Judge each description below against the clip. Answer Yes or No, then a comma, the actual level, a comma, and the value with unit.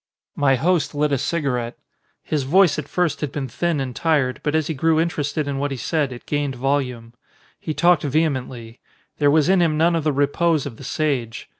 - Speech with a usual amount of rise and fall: Yes, average, 3.1 semitones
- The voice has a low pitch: No, medium, 145 Hz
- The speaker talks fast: Yes, fast, 210 wpm